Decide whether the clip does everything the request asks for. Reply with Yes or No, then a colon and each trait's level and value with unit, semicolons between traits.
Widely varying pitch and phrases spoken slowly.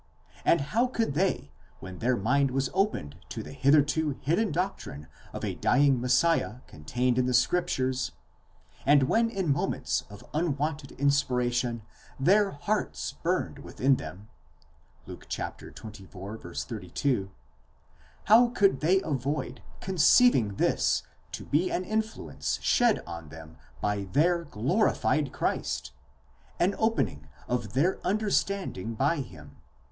Yes: wide, 7.9 semitones; slow, 125 wpm